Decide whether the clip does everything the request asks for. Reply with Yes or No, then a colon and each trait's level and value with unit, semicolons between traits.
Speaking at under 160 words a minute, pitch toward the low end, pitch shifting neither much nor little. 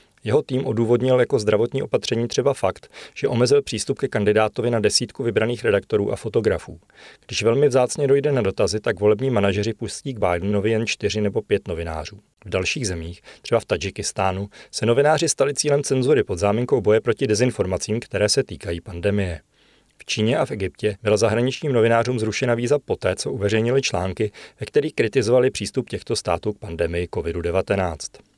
No: average, 165 wpm; low, 110 Hz; average, 4.1 semitones